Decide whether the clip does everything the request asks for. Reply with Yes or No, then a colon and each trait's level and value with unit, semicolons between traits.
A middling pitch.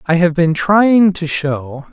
Yes: medium, 170 Hz